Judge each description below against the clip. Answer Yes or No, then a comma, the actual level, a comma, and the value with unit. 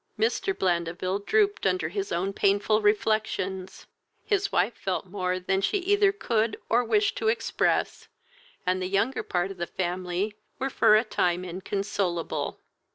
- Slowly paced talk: No, average, 150 wpm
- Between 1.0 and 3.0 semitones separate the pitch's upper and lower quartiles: No, average, 3.9 semitones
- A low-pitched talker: No, high, 195 Hz